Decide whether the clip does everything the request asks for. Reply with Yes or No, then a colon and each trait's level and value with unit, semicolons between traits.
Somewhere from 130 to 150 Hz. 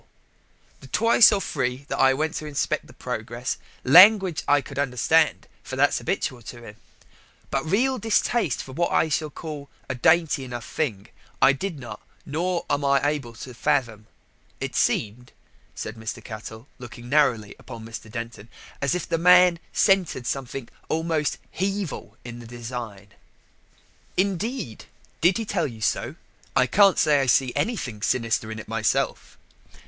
Yes: medium, 140 Hz